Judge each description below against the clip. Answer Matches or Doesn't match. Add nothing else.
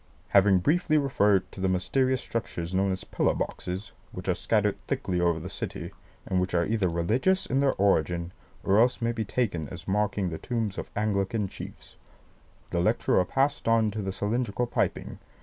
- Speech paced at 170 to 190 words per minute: Matches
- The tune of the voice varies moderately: Matches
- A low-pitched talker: Matches